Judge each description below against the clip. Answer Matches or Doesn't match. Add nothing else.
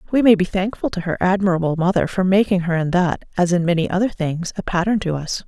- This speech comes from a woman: Matches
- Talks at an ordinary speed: Doesn't match